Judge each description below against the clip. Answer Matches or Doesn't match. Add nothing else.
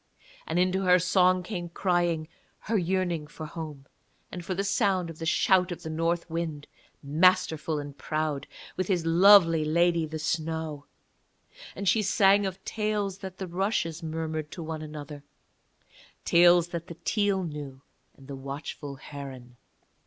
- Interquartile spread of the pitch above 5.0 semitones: Doesn't match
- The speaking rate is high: Doesn't match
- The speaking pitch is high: Doesn't match